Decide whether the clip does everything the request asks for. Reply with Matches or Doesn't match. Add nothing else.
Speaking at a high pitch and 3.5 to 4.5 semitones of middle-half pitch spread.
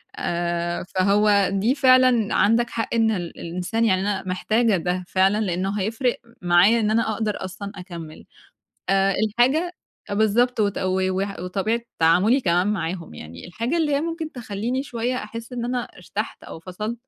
Matches